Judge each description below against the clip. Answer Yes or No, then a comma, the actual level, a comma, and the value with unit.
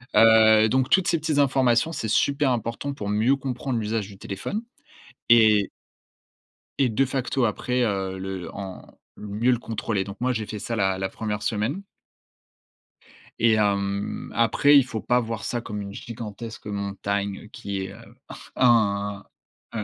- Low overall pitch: Yes, low, 110 Hz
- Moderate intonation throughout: Yes, average, 3.5 semitones